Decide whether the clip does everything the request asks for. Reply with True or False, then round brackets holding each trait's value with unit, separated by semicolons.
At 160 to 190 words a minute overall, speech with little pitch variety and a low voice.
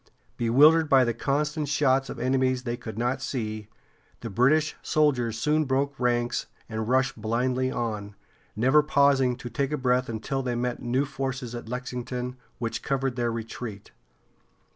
False (150 wpm; 2.3 semitones; 125 Hz)